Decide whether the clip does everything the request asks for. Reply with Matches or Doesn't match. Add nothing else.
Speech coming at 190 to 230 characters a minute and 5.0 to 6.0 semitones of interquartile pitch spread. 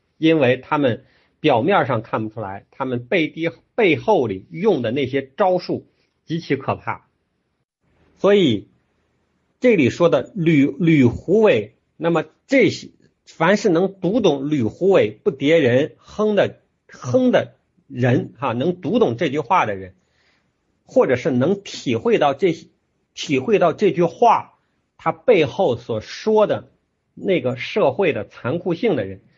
Doesn't match